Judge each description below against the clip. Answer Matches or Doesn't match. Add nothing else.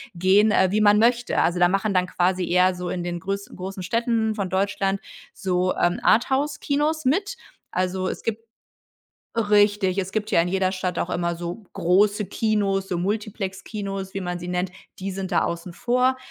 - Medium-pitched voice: Doesn't match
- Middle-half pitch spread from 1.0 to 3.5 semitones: Matches